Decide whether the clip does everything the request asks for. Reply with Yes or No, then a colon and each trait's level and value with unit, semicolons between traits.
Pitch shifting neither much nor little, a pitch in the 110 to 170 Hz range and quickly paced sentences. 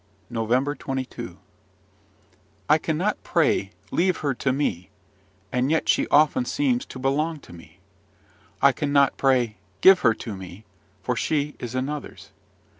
No: average, 4.0 semitones; medium, 140 Hz; slow, 135 wpm